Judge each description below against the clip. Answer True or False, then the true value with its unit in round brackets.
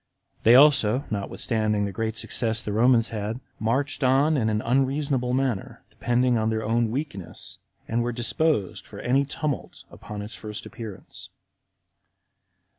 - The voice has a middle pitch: False (115 Hz)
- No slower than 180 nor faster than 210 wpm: False (140 wpm)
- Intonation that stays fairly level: False (3.4 semitones)